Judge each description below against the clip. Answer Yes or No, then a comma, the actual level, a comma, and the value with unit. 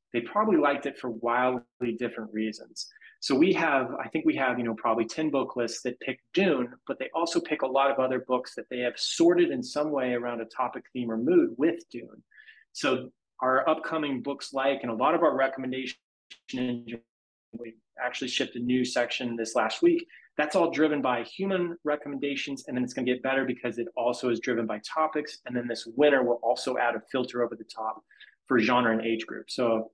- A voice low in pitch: Yes, low, 125 Hz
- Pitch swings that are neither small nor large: Yes, average, 3.7 semitones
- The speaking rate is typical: No, fast, 210 wpm